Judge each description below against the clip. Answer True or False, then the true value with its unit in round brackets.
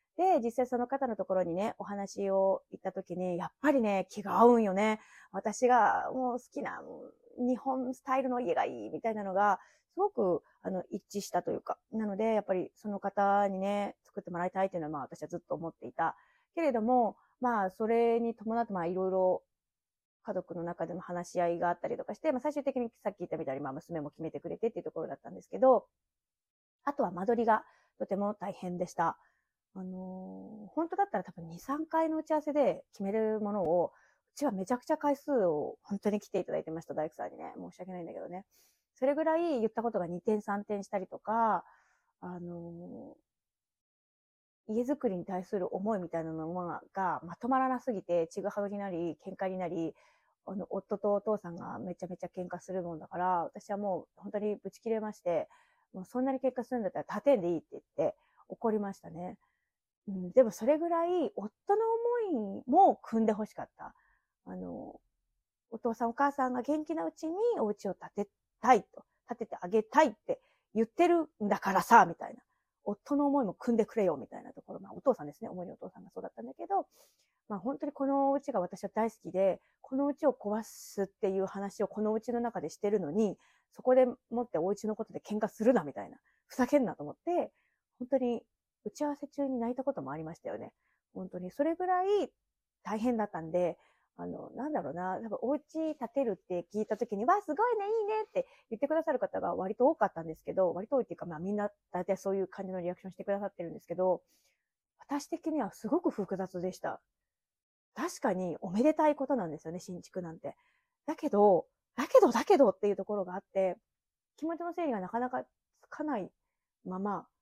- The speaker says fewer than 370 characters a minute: False (395 characters per minute)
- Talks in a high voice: True (210 Hz)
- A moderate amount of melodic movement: False (6.3 semitones)